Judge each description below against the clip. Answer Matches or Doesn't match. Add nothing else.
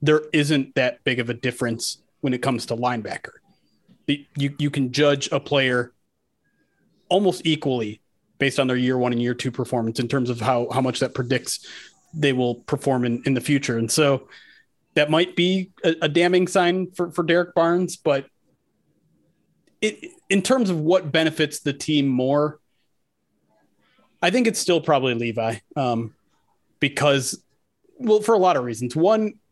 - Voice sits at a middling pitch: Matches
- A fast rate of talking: Doesn't match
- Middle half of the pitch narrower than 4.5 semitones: Doesn't match